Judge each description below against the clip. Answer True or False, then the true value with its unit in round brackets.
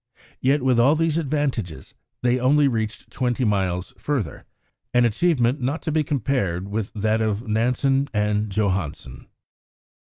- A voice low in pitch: True (120 Hz)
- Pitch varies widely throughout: False (4.8 semitones)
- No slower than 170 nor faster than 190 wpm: False (135 wpm)